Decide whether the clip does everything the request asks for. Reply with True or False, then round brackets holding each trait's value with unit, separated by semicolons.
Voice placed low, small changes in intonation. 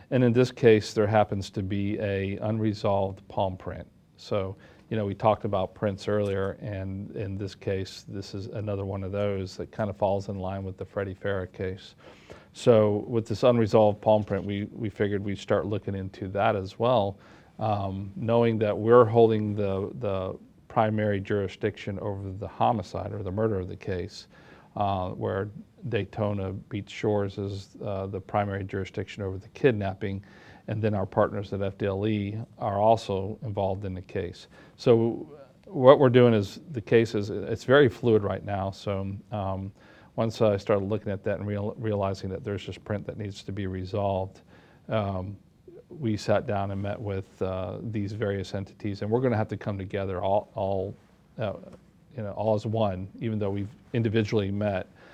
True (100 Hz; 1.9 semitones)